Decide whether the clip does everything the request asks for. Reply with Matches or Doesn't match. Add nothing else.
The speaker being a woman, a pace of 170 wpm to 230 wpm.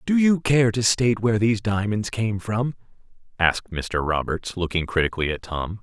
Doesn't match